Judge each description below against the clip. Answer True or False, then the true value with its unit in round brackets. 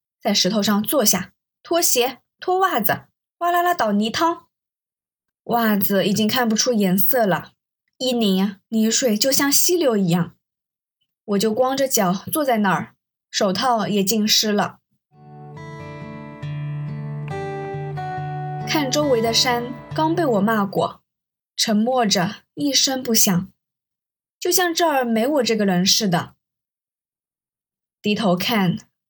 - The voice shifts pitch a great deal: True (5.8 semitones)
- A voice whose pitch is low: False (215 Hz)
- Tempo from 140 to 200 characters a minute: True (170 characters per minute)